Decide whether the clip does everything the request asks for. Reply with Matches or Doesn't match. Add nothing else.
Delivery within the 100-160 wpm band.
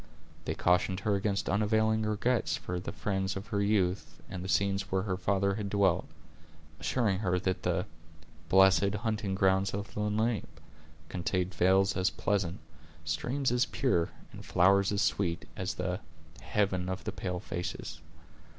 Matches